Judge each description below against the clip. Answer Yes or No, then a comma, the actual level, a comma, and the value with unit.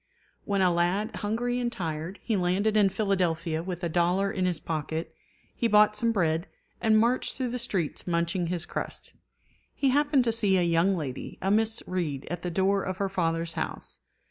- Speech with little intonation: No, average, 4.2 semitones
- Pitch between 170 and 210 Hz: Yes, high, 190 Hz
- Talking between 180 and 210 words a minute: Yes, average, 195 wpm